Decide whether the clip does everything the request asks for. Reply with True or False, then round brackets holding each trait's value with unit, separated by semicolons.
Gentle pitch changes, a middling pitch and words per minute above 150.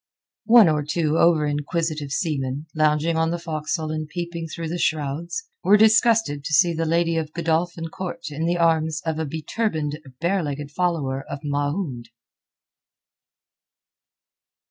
False (2.3 semitones; 160 Hz; 145 wpm)